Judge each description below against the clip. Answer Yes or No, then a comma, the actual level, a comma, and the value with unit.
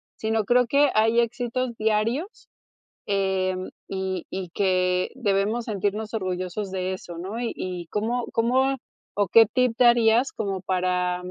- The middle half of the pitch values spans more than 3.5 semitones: Yes, average, 4.0 semitones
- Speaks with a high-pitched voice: Yes, high, 210 Hz